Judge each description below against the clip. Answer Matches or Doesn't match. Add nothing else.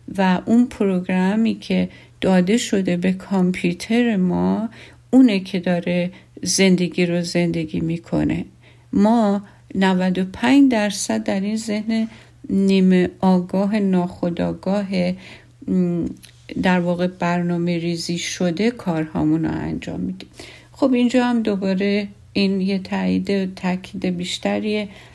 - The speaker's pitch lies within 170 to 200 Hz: Matches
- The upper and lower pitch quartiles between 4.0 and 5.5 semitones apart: Doesn't match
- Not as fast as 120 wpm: Matches